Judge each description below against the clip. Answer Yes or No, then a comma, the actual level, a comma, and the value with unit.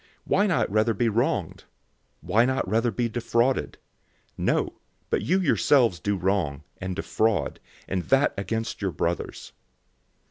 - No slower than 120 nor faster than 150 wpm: Yes, average, 140 wpm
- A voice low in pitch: Yes, low, 110 Hz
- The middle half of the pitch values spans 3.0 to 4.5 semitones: Yes, average, 4.2 semitones